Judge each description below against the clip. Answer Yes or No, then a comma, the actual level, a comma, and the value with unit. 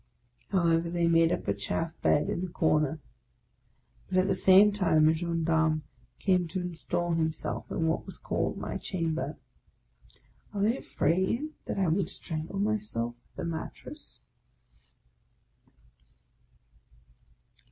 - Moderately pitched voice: Yes, medium, 170 Hz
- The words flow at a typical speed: No, slow, 130 wpm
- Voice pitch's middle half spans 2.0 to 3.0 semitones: Yes, average, 2.7 semitones